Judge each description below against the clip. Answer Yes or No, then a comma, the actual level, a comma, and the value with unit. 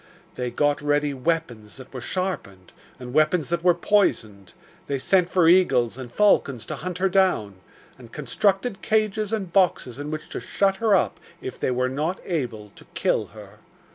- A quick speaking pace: No, average, 175 wpm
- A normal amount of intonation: No, wide, 7.1 semitones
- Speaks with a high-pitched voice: No, medium, 155 Hz